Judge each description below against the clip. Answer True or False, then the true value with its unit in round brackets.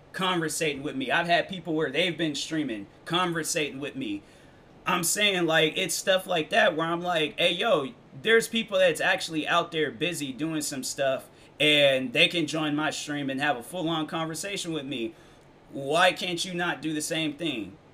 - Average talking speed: True (185 wpm)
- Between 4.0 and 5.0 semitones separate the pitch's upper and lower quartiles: False (2.9 semitones)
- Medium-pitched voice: True (160 Hz)